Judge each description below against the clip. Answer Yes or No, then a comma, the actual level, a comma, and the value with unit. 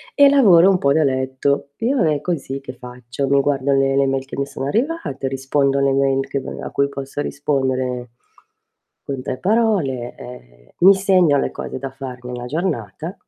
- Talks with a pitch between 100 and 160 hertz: Yes, medium, 140 Hz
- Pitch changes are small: No, average, 3.3 semitones